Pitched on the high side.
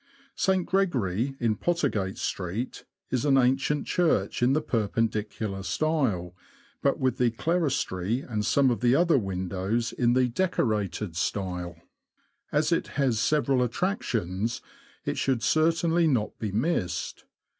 No: low, 120 Hz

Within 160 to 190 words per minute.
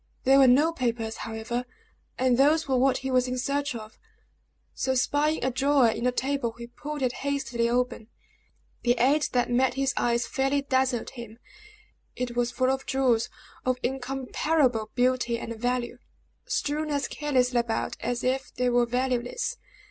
Yes: average, 165 wpm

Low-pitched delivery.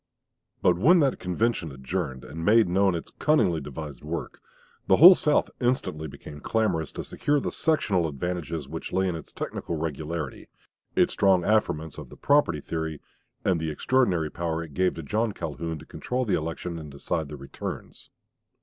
Yes: very low, 85 Hz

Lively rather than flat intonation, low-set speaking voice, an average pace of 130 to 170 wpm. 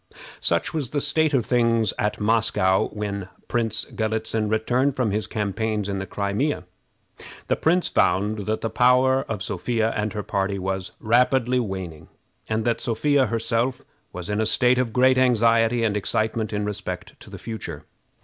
No: average, 3.1 semitones; low, 110 Hz; average, 165 wpm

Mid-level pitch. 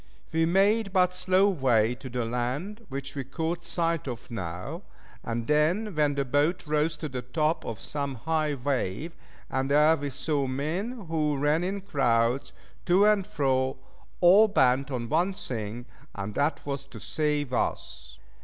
Yes: medium, 145 Hz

